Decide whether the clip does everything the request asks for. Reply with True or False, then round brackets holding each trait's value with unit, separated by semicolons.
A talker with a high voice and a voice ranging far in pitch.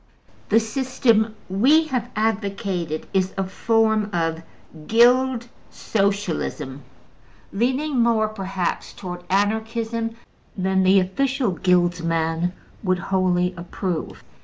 False (200 Hz; 4.0 semitones)